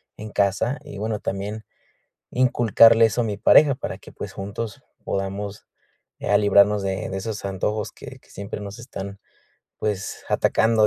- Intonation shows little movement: Yes, narrow, 2.2 semitones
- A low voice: Yes, low, 105 Hz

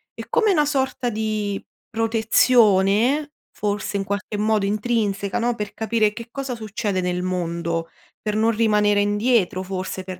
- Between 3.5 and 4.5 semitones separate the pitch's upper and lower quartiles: No, average, 2.7 semitones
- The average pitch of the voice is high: Yes, high, 210 Hz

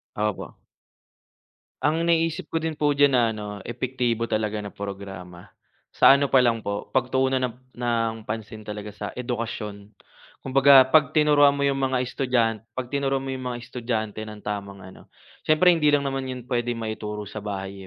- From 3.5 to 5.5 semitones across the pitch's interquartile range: Yes, average, 4.2 semitones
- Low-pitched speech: Yes, low, 120 Hz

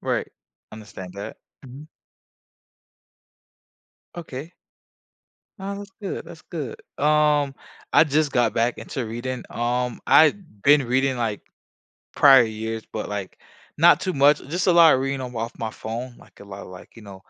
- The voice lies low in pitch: Yes, low, 130 Hz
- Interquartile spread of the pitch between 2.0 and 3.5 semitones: No, average, 5.1 semitones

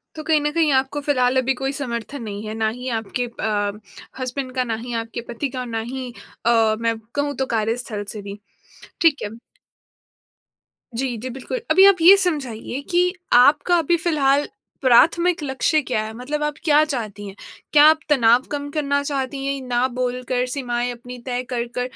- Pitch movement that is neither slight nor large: Yes, average, 3.7 semitones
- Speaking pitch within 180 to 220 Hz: No, very high, 255 Hz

